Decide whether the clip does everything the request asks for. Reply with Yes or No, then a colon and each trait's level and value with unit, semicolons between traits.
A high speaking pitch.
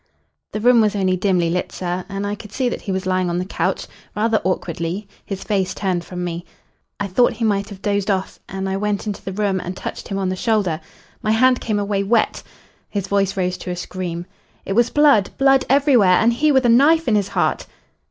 Yes: high, 200 Hz